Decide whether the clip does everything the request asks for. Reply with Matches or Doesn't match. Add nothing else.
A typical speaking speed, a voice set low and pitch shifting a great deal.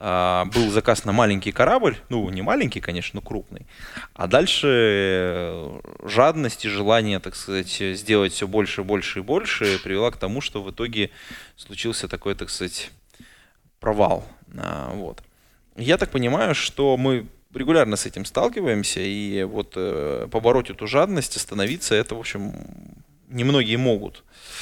Doesn't match